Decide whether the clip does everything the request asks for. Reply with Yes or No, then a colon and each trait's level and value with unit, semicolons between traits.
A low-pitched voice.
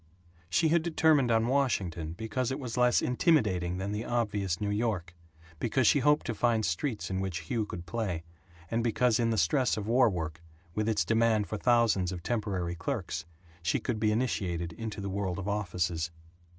Yes: low, 105 Hz